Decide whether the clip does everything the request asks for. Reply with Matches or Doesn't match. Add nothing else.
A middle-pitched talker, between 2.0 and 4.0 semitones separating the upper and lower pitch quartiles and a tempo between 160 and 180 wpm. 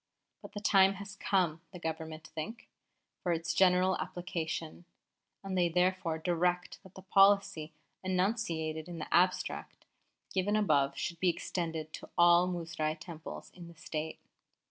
Doesn't match